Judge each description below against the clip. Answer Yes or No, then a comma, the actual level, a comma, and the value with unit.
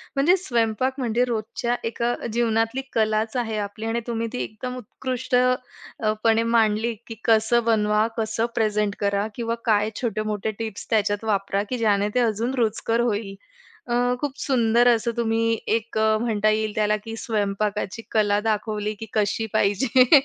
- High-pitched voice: Yes, high, 225 Hz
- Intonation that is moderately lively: No, narrow, 1.8 semitones